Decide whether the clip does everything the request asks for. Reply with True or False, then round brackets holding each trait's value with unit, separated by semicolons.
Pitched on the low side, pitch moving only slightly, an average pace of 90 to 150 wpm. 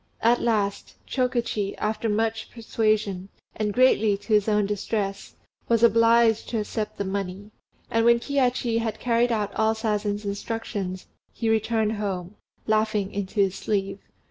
False (215 Hz; 2.1 semitones; 145 wpm)